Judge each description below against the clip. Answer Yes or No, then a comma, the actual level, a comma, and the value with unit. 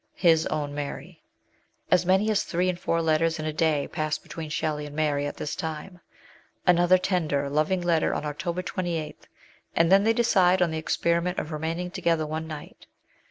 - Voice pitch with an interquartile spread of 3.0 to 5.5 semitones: No, narrow, 2.6 semitones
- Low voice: No, medium, 165 Hz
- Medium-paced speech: Yes, average, 180 wpm